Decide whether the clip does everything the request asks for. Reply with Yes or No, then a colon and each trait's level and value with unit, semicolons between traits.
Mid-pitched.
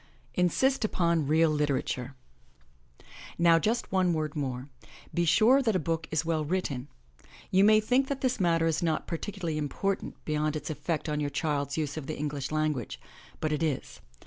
Yes: medium, 160 Hz